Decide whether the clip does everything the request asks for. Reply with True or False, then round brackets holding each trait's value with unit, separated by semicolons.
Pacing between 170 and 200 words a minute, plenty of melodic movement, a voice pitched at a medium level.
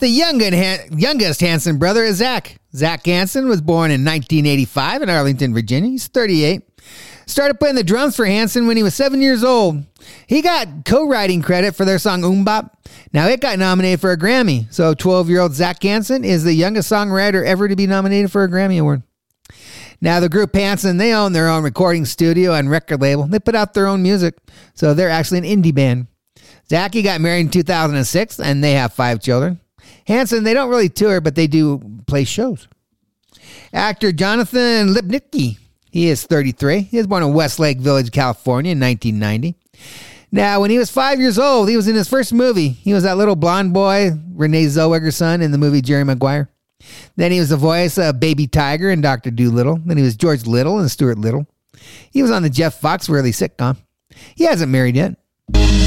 True (190 wpm; 5.9 semitones; 175 Hz)